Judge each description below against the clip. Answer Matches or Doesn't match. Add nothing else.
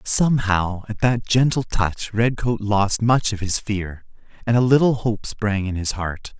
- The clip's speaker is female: Doesn't match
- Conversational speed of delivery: Matches